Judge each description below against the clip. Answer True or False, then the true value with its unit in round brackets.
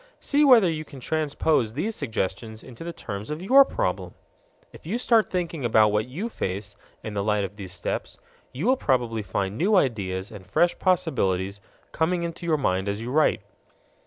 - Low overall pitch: True (125 Hz)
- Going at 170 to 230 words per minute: True (185 wpm)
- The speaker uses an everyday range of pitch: False (8.8 semitones)